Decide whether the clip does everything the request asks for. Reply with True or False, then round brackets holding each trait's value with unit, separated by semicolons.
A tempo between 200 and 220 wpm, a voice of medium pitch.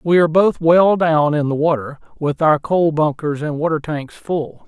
True (205 wpm; 155 Hz)